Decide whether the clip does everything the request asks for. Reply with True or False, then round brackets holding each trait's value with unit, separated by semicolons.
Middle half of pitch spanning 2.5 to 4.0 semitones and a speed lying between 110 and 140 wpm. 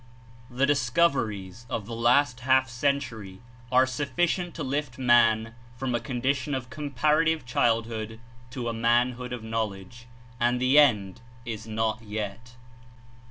True (2.9 semitones; 135 wpm)